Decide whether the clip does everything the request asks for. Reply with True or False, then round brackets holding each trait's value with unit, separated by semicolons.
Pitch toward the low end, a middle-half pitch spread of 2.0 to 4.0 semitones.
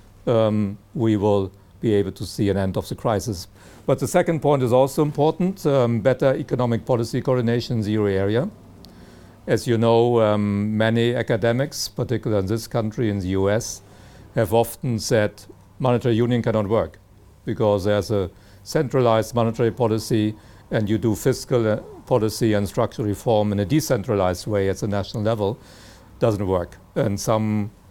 True (110 Hz; 2.9 semitones)